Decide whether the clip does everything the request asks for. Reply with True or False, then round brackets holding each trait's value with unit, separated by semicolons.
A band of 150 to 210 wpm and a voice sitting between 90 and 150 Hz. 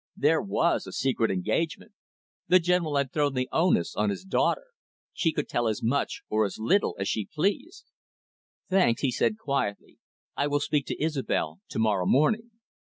True (170 wpm; 140 Hz)